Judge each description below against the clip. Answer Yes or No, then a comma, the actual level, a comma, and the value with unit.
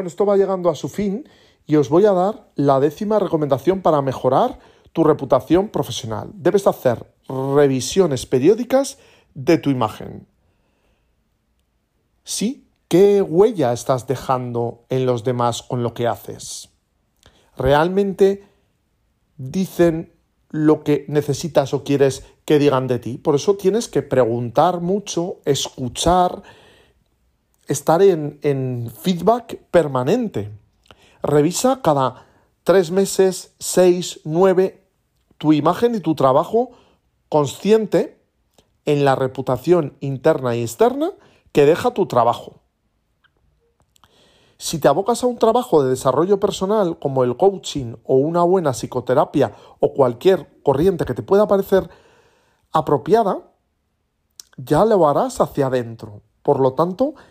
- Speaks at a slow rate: Yes, slow, 120 wpm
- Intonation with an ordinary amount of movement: No, wide, 6.7 semitones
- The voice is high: No, medium, 155 Hz